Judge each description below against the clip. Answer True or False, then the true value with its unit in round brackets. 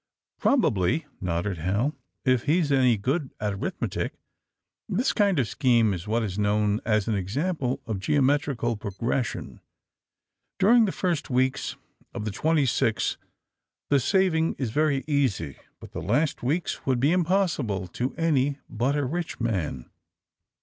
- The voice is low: True (130 Hz)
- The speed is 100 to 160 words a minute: True (150 wpm)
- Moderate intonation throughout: False (6.4 semitones)